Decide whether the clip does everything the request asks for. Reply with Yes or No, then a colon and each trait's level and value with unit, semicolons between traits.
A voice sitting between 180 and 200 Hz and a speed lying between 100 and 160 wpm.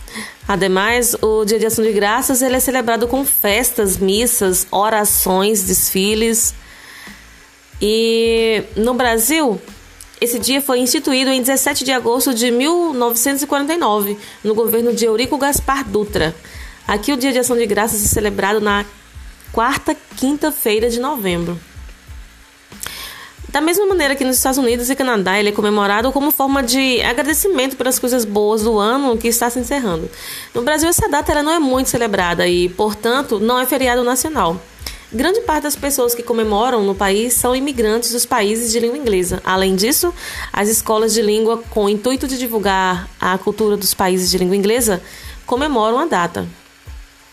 No: high, 235 Hz; average, 155 wpm